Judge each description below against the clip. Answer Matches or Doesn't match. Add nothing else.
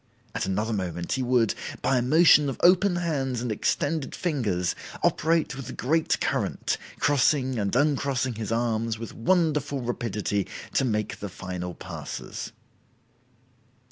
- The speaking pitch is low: Matches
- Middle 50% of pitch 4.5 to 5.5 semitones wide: Matches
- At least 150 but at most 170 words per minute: Doesn't match